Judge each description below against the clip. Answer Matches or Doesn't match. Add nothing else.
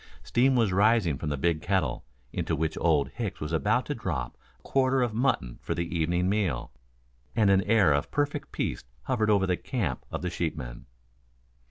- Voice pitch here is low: Matches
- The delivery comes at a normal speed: Matches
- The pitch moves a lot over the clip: Matches